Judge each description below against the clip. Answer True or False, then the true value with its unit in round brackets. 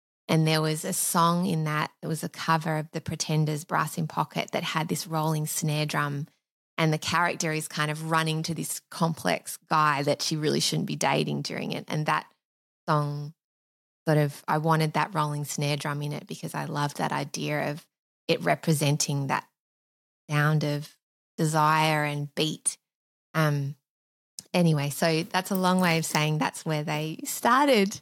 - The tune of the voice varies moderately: False (1.7 semitones)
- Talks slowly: False (175 wpm)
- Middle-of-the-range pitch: True (155 Hz)